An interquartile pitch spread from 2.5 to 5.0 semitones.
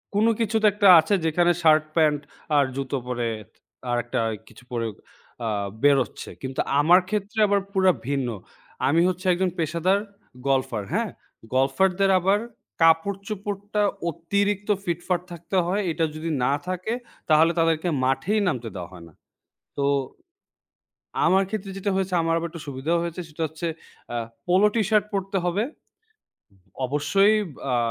No: wide, 5.4 semitones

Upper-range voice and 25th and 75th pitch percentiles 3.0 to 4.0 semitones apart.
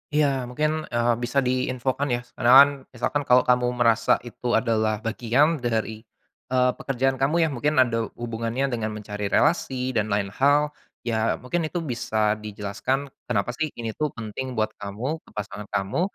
No: low, 120 Hz; average, 3.4 semitones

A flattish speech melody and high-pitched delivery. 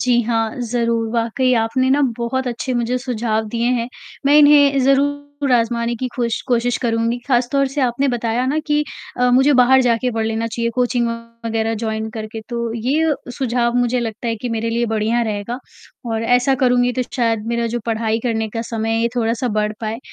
Yes: narrow, 1.9 semitones; high, 235 Hz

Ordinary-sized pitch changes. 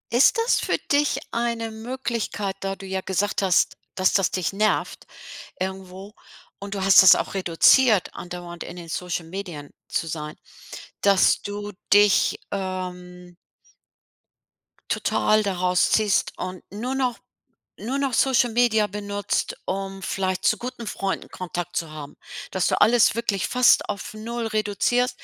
Yes: average, 3.6 semitones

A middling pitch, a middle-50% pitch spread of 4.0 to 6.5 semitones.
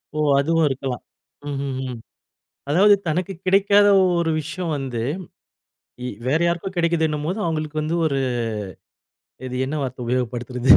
Yes: medium, 155 Hz; average, 4.4 semitones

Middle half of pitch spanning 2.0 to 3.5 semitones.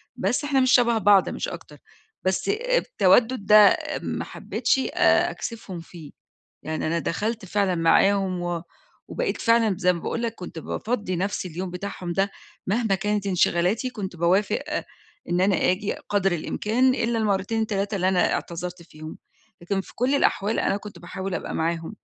No: average, 4.0 semitones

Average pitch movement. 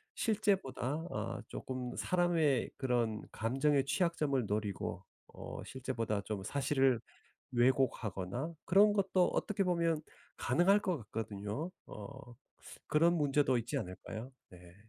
No: wide, 6.9 semitones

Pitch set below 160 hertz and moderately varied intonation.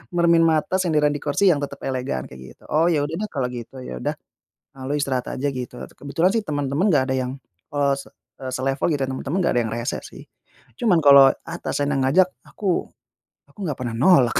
Yes: medium, 140 Hz; average, 3.9 semitones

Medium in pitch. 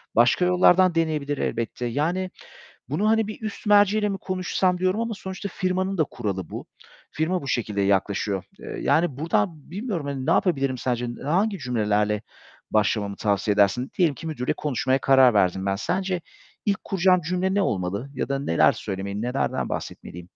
Yes: medium, 145 Hz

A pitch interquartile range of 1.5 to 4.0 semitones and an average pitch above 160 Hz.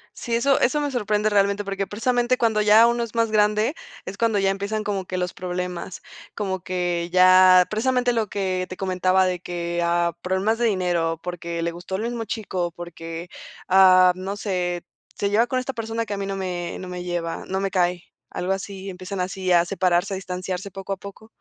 Yes: average, 2.8 semitones; high, 190 Hz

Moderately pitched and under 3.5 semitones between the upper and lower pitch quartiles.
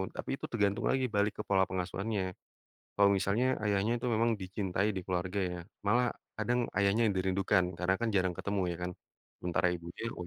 No: low, 100 Hz; narrow, 2.6 semitones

